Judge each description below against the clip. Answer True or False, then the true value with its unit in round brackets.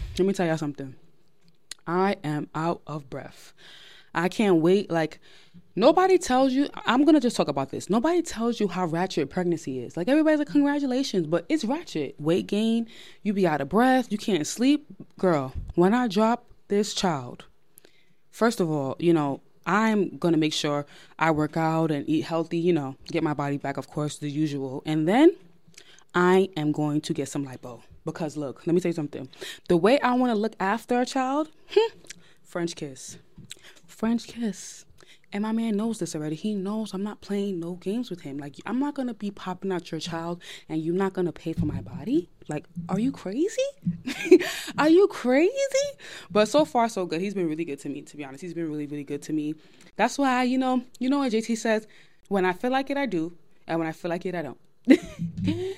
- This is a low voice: False (180 Hz)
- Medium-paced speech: False (210 wpm)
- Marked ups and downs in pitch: True (6.5 semitones)